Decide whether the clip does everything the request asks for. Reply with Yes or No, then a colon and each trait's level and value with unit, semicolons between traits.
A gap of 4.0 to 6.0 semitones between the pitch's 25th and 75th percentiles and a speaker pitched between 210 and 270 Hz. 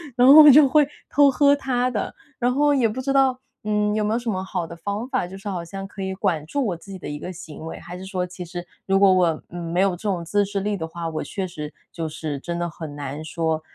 No: average, 5.0 semitones; high, 190 Hz